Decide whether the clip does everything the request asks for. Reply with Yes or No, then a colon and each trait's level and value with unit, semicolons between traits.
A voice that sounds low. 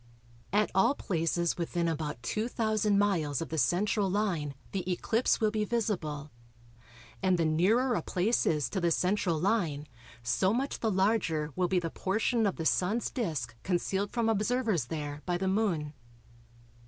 No: medium, 185 Hz